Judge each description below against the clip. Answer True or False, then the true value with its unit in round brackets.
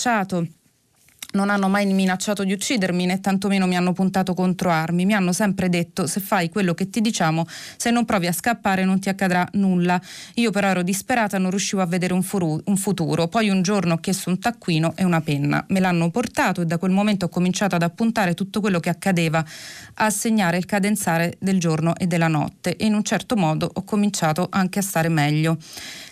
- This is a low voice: False (185 Hz)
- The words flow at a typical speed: False (200 wpm)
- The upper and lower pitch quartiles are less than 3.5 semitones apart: True (3.0 semitones)